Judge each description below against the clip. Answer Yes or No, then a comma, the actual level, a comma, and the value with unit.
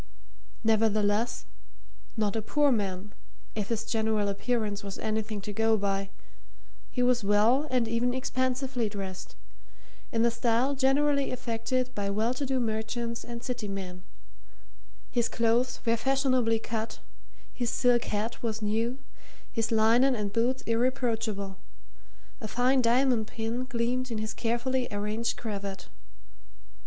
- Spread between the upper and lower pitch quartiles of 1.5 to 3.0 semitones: Yes, narrow, 2.6 semitones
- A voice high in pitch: Yes, high, 230 Hz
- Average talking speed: No, slow, 130 wpm